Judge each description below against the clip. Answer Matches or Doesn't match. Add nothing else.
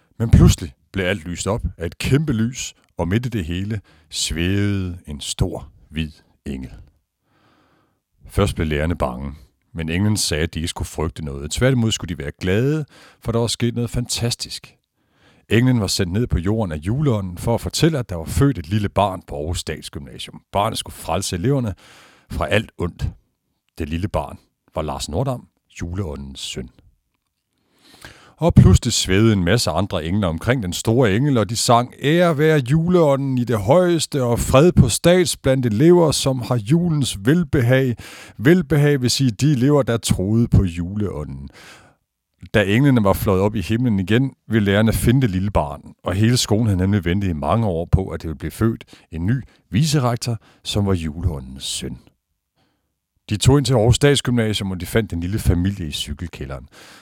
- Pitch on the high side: Doesn't match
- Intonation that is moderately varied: Doesn't match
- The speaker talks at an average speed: Matches